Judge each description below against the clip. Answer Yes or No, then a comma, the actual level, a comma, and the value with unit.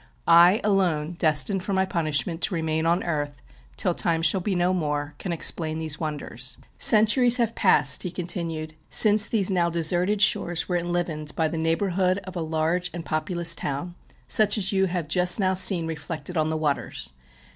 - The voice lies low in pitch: No, medium, 170 Hz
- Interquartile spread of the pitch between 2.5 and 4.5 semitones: Yes, average, 2.9 semitones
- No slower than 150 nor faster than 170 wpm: No, average, 180 wpm